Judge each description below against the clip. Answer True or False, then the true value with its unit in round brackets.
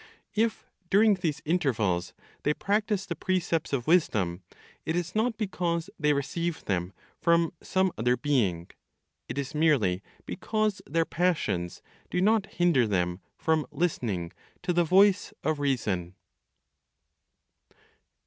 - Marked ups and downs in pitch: True (7.9 semitones)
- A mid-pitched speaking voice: True (160 Hz)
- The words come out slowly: True (125 wpm)